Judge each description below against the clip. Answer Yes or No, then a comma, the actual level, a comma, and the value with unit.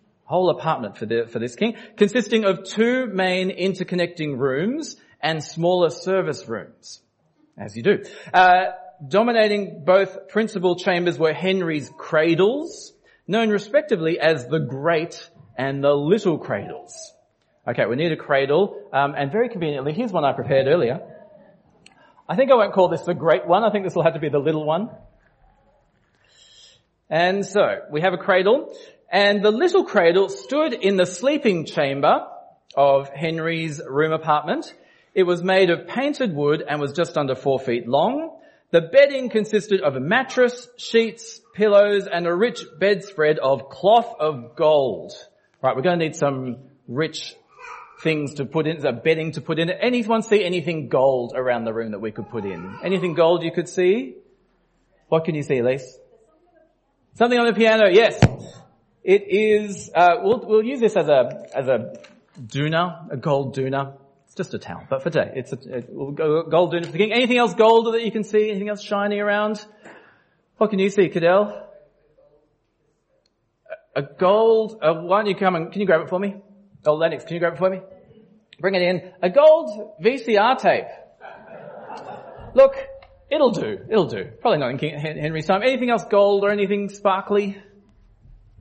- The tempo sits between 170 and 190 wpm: Yes, average, 175 wpm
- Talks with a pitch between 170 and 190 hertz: Yes, medium, 185 Hz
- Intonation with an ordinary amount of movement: No, wide, 5.8 semitones